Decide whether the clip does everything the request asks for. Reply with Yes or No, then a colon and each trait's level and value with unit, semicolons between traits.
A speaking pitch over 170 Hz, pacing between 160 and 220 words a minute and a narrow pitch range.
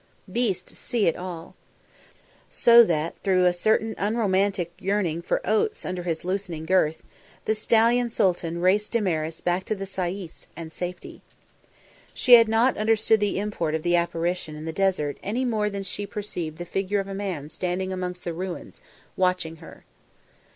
No: medium, 185 Hz; average, 170 wpm; average, 3.4 semitones